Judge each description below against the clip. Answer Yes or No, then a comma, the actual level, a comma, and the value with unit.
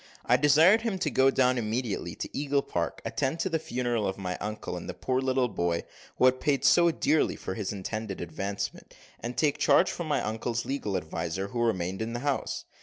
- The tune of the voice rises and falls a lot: Yes, wide, 5.9 semitones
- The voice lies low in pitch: Yes, low, 120 Hz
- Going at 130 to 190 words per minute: No, fast, 205 wpm